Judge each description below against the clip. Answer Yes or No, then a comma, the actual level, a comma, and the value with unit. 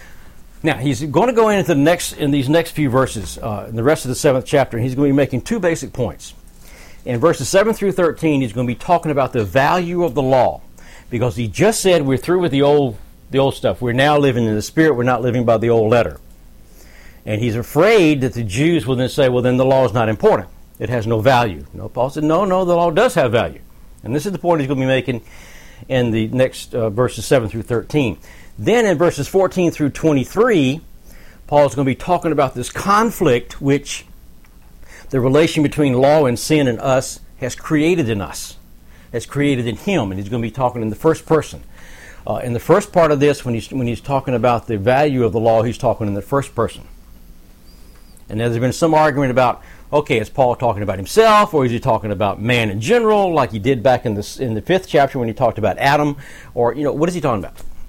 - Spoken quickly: Yes, fast, 235 wpm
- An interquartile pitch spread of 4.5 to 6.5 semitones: Yes, average, 5.1 semitones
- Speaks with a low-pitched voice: Yes, low, 130 Hz